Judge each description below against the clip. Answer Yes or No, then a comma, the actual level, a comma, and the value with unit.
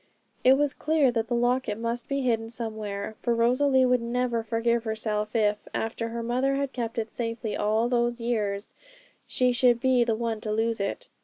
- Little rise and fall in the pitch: Yes, narrow, 1.9 semitones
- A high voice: Yes, high, 235 Hz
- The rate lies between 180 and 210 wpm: Yes, average, 185 wpm